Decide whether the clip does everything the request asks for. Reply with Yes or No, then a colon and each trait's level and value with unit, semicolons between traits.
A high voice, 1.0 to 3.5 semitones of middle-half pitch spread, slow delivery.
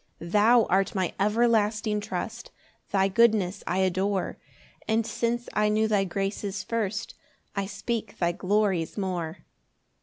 Yes: high, 205 Hz; narrow, 2.5 semitones; slow, 130 wpm